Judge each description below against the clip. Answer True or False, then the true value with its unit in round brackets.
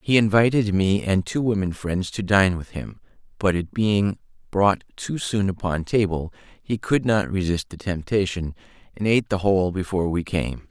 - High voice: False (95 Hz)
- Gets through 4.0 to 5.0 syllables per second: True (4.8 syllables/s)